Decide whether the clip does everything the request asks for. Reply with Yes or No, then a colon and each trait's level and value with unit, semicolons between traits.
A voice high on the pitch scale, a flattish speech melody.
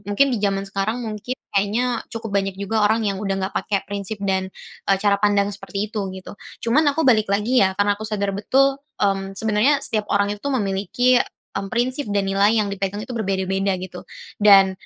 Yes: high, 205 Hz; narrow, 2.2 semitones